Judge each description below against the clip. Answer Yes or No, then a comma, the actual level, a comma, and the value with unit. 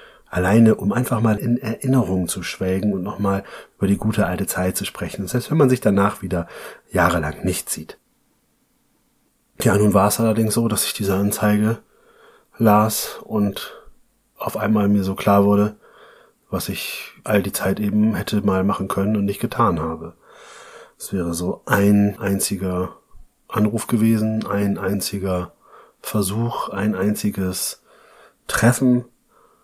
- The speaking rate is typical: Yes, average, 145 wpm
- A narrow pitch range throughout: Yes, narrow, 2.1 semitones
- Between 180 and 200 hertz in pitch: No, low, 105 Hz